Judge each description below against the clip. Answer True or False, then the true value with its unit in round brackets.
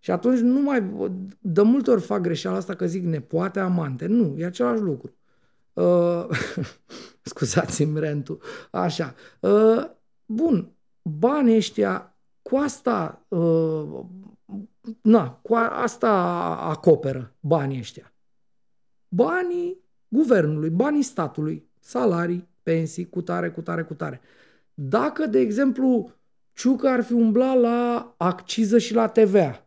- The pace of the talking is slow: False (125 wpm)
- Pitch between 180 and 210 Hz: True (190 Hz)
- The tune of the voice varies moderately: False (7.2 semitones)